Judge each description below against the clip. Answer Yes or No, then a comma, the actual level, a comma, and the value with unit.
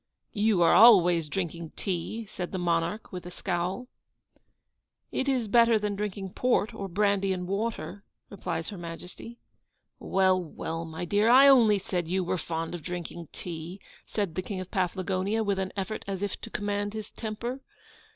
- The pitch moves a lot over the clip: No, average, 3.3 semitones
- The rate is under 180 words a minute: Yes, average, 170 wpm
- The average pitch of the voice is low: No, high, 195 Hz